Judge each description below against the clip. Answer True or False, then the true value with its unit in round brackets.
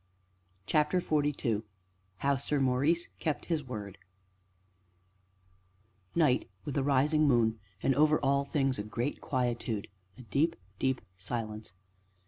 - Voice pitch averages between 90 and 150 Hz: True (135 Hz)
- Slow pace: True (115 wpm)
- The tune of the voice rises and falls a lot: False (3.9 semitones)